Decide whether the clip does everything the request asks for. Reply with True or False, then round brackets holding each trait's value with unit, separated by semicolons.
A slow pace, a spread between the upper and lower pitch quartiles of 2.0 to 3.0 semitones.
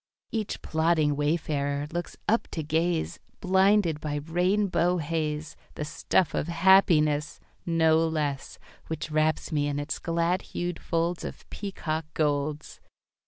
True (125 wpm; 2.5 semitones)